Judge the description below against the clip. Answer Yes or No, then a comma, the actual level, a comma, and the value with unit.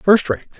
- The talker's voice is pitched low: No, medium, 165 Hz